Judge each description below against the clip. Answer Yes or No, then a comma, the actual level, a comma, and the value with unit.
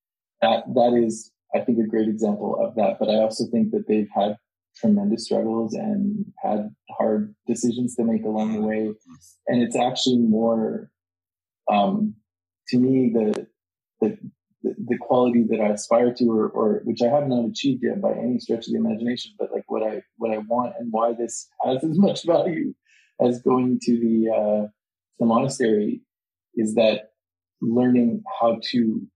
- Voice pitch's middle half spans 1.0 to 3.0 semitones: Yes, narrow, 2.4 semitones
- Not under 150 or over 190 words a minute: Yes, average, 170 wpm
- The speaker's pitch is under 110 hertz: No, low, 115 Hz